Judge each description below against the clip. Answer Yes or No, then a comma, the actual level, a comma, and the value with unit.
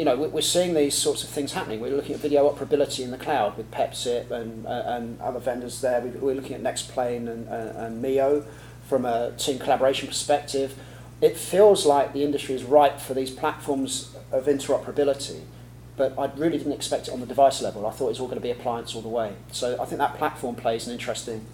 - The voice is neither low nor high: No, low, 130 Hz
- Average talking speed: No, fast, 225 wpm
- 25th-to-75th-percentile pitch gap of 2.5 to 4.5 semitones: Yes, average, 2.9 semitones